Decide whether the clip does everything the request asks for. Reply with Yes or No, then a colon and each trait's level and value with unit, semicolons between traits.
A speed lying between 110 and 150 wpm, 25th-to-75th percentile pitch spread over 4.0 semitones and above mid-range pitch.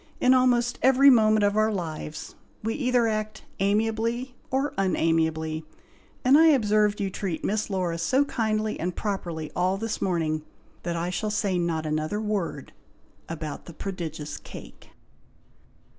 Yes: average, 145 wpm; average, 5.0 semitones; high, 205 Hz